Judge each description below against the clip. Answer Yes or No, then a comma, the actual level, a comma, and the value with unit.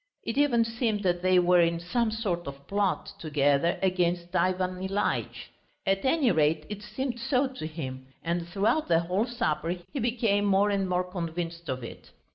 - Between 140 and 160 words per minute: No, average, 175 wpm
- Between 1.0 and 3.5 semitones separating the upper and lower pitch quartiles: No, average, 4.4 semitones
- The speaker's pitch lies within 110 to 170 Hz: No, medium, 185 Hz